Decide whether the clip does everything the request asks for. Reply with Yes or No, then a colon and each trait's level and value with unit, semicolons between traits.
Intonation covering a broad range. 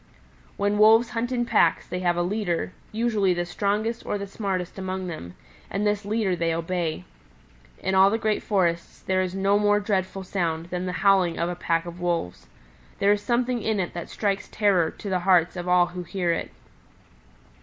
No: average, 2.9 semitones